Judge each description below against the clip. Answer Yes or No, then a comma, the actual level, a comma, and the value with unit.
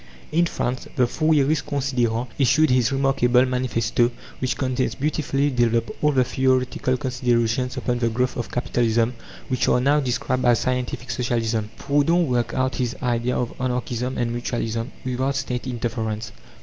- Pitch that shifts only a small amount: Yes, narrow, 1.8 semitones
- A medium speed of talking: Yes, average, 150 wpm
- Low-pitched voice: Yes, low, 125 Hz